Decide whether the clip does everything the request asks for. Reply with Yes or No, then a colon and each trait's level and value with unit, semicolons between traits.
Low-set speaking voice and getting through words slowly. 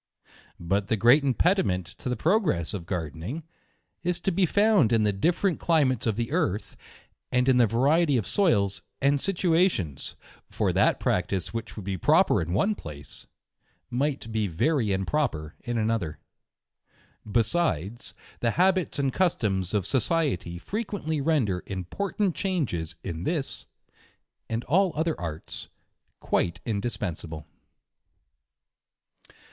Yes: low, 120 Hz; slow, 130 wpm